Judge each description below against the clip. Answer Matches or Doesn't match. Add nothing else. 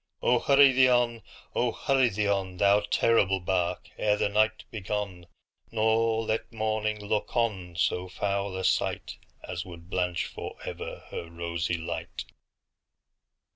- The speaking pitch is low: Matches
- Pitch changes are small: Doesn't match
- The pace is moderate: Doesn't match